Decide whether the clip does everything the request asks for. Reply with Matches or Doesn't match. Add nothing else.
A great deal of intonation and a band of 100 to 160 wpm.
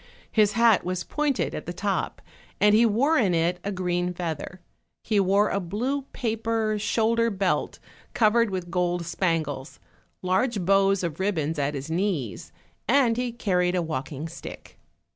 Doesn't match